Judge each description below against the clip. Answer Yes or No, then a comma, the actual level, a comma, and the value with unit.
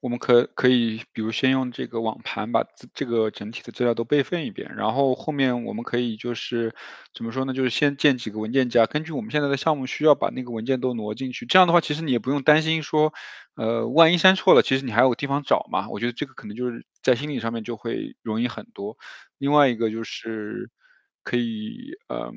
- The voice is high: No, low, 130 Hz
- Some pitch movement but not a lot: Yes, average, 4.1 semitones